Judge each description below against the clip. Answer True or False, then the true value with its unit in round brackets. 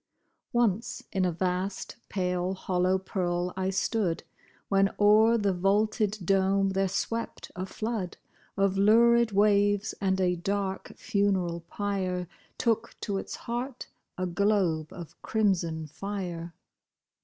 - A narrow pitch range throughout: True (2.3 semitones)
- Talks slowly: True (120 wpm)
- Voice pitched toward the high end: True (195 Hz)